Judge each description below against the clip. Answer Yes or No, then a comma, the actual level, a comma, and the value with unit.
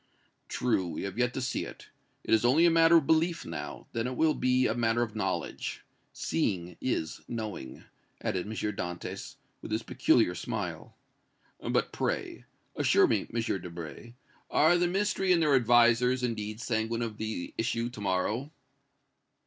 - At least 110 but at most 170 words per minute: Yes, average, 160 wpm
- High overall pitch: No, low, 120 Hz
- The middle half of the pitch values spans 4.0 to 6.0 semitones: No, average, 3.6 semitones